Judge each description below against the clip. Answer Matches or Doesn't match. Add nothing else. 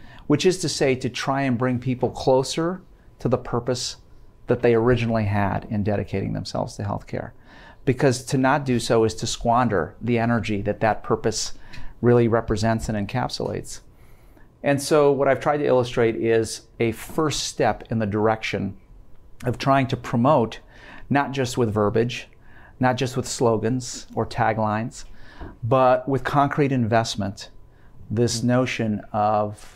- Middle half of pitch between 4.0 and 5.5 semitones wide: Doesn't match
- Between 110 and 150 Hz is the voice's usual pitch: Matches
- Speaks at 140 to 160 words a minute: Matches